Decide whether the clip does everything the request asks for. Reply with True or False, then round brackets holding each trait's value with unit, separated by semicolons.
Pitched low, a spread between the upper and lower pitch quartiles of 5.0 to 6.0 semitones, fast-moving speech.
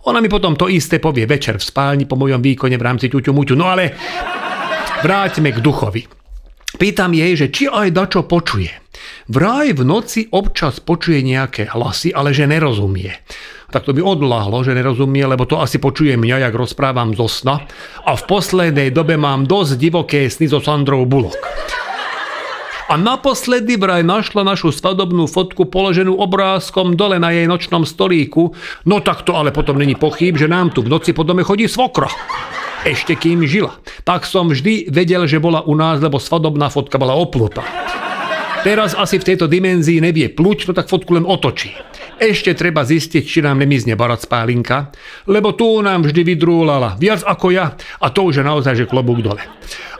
False (160 Hz; 5.4 semitones; 175 wpm)